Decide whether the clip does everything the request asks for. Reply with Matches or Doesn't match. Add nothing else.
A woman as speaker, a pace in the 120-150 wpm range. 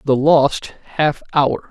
Doesn't match